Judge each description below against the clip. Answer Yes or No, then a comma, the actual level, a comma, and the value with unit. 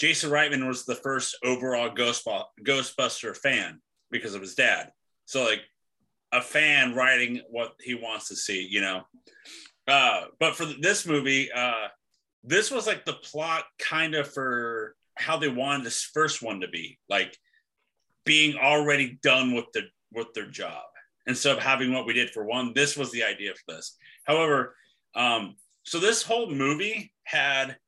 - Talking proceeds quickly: No, average, 165 wpm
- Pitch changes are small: No, average, 3.7 semitones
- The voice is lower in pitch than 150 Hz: Yes, low, 135 Hz